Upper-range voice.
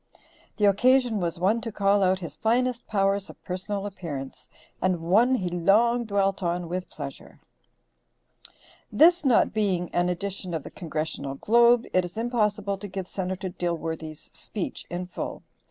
Yes: high, 195 Hz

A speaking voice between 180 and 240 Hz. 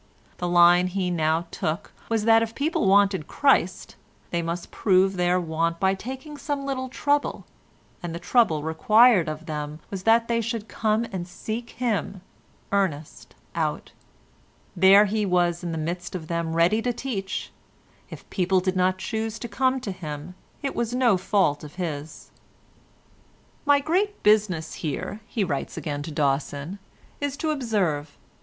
Yes: high, 190 Hz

